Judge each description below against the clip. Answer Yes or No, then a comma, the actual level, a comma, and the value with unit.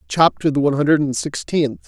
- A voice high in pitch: No, medium, 145 Hz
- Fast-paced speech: No, average, 190 wpm